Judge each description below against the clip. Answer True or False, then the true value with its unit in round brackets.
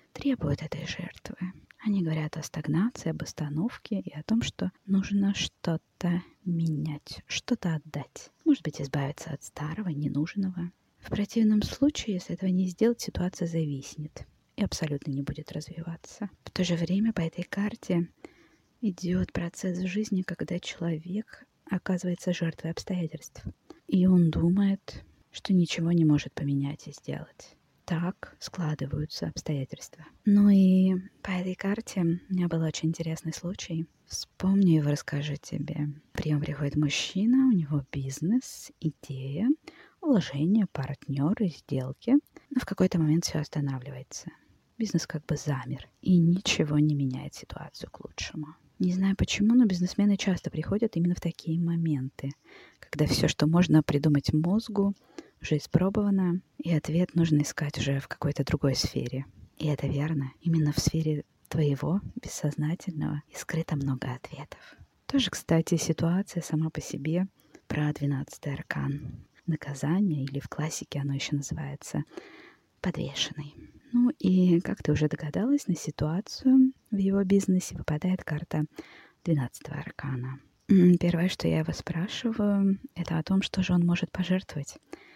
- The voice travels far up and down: False (4.1 semitones)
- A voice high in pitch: False (165 Hz)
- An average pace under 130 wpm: False (135 wpm)